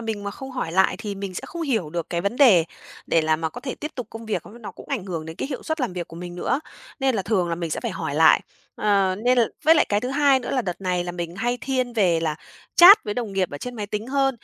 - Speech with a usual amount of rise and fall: No, wide, 6.2 semitones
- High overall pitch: Yes, high, 205 Hz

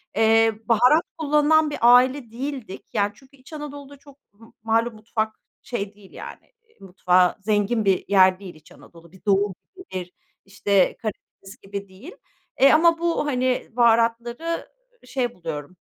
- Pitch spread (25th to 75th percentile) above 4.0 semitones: Yes, wide, 5.6 semitones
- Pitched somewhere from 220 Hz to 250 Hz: Yes, high, 225 Hz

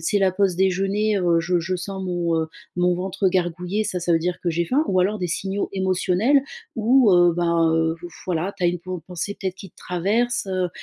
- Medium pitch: Yes, medium, 180 Hz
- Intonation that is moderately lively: No, narrow, 1.9 semitones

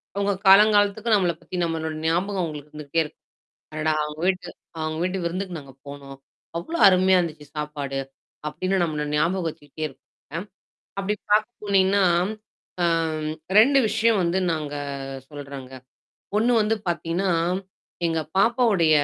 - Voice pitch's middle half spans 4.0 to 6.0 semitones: Yes, average, 4.3 semitones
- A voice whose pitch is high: No, medium, 170 Hz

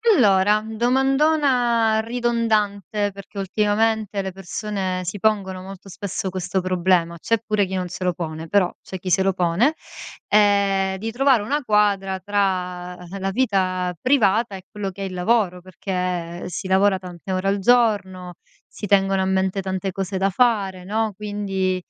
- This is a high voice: Yes, high, 195 Hz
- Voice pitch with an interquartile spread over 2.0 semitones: Yes, narrow, 2.4 semitones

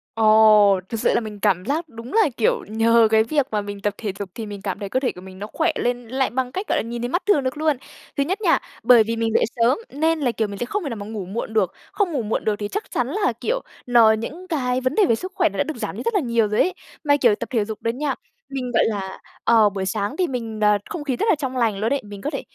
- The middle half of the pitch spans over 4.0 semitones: Yes, average, 5.2 semitones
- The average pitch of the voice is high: Yes, high, 235 Hz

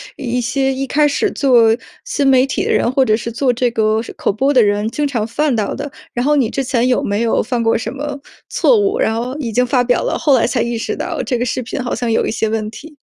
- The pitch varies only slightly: No, average, 3.2 semitones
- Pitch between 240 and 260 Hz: Yes, high, 245 Hz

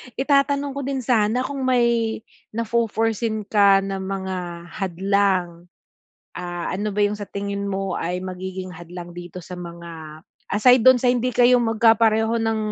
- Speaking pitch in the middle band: No, high, 205 Hz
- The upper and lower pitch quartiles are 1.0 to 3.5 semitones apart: No, average, 4.1 semitones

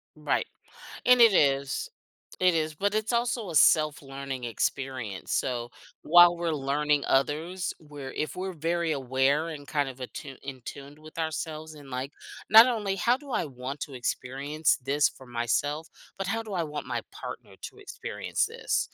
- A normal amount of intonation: Yes, average, 4.4 semitones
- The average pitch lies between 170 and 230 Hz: No, medium, 150 Hz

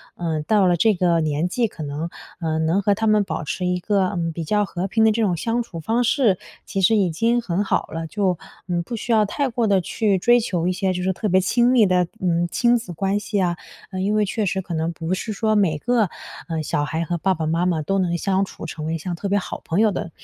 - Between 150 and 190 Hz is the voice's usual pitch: Yes, medium, 185 Hz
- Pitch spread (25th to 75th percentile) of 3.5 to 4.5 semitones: Yes, average, 3.9 semitones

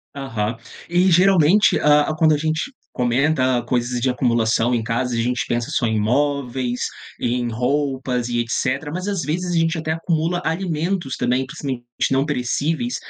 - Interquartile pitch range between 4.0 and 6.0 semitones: Yes, average, 4.7 semitones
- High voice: No, low, 135 Hz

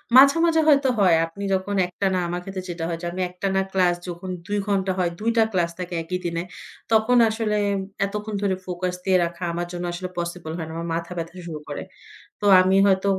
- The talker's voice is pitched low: No, medium, 185 Hz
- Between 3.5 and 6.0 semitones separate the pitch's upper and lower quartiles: No, average, 2.7 semitones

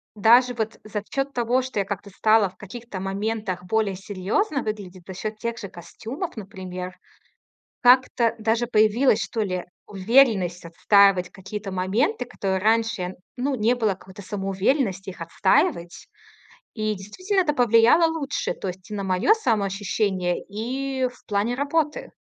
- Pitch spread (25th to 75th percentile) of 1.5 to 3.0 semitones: No, average, 4.3 semitones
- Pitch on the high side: Yes, high, 215 Hz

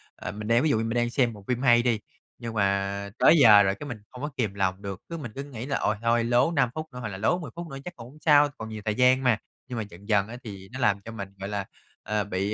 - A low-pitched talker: Yes, low, 115 Hz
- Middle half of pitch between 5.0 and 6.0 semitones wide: No, average, 4.0 semitones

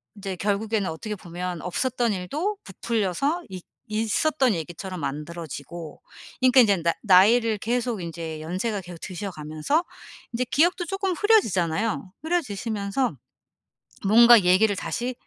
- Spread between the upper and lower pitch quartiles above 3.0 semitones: Yes, wide, 5.6 semitones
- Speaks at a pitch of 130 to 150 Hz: No, high, 205 Hz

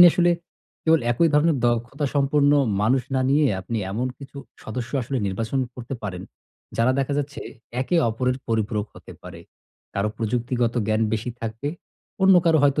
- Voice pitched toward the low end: Yes, low, 125 Hz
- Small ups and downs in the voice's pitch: No, average, 4.2 semitones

